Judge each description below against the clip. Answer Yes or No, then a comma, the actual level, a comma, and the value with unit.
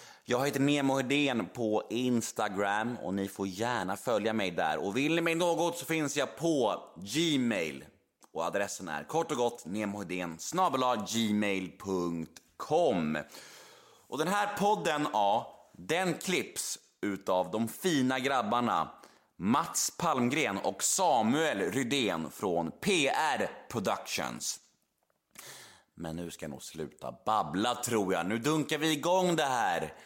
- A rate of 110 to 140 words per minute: Yes, average, 130 wpm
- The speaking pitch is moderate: No, low, 125 Hz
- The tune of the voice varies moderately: No, wide, 8.0 semitones